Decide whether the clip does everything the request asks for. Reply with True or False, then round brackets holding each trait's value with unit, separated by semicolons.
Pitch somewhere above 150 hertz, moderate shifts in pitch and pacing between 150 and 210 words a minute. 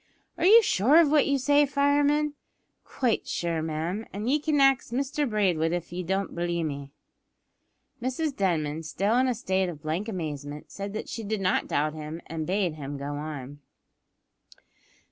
False (190 Hz; 8.9 semitones; 165 wpm)